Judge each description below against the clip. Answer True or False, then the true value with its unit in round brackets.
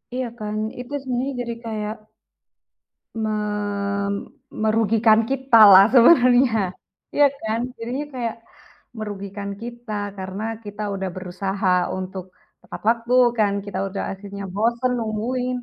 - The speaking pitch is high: True (220 Hz)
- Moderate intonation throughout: True (3.3 semitones)